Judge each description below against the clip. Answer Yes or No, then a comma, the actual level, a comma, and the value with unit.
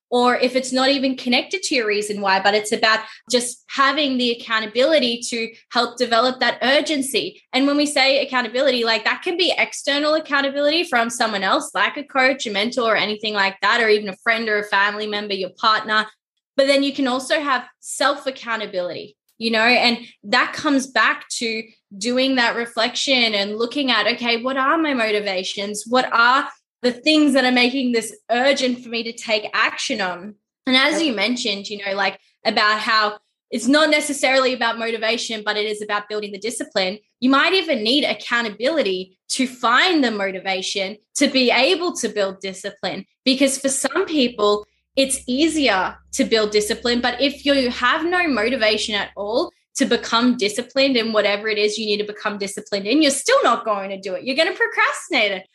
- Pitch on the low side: No, high, 235 Hz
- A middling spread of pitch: Yes, average, 4.2 semitones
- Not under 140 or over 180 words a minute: No, average, 190 wpm